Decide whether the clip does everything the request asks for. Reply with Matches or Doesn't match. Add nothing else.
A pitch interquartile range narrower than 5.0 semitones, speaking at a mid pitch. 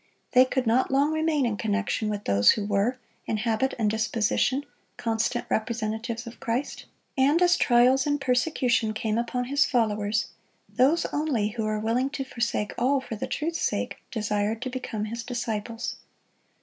Doesn't match